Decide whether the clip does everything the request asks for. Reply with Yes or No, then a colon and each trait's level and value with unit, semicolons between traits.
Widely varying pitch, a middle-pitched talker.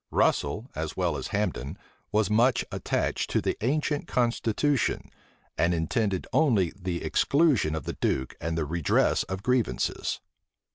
No: wide, 7.2 semitones; low, 100 Hz